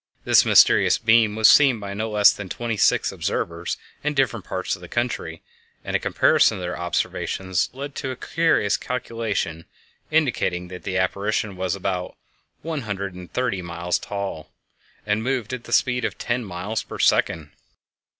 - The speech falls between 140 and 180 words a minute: Yes, average, 170 wpm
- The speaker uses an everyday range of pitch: Yes, average, 4.7 semitones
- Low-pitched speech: Yes, low, 105 Hz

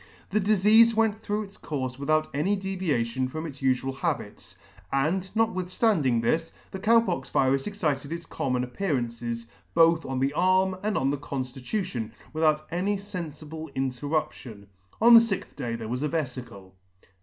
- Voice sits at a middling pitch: Yes, medium, 155 Hz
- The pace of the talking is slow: No, average, 180 wpm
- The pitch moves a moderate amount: No, wide, 6.6 semitones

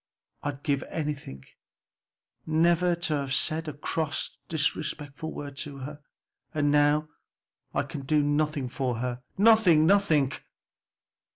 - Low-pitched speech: No, medium, 150 Hz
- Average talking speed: No, slow, 125 wpm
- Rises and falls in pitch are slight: Yes, narrow, 2.0 semitones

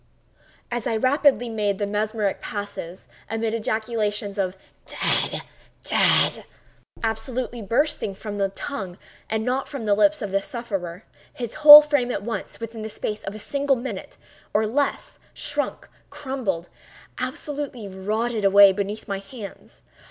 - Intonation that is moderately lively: Yes, average, 3.7 semitones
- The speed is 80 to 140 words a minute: Yes, slow, 135 wpm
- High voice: Yes, high, 220 Hz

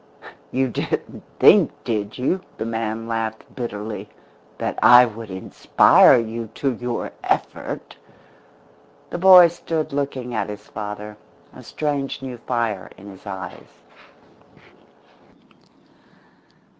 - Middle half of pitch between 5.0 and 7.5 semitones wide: No, average, 3.8 semitones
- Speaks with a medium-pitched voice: No, low, 115 Hz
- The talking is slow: Yes, slow, 110 wpm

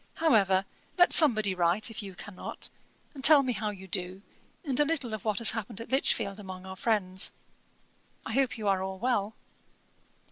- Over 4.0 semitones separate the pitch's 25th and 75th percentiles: Yes, average, 4.4 semitones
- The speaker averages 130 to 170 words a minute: No, average, 180 wpm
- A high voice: Yes, high, 210 Hz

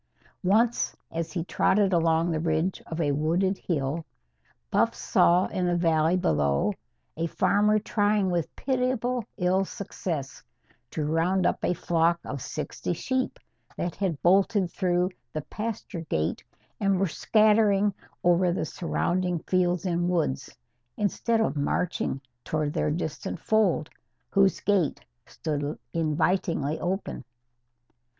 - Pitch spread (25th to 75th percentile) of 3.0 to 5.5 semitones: Yes, average, 3.5 semitones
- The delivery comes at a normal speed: No, slow, 130 wpm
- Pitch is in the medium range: Yes, medium, 175 Hz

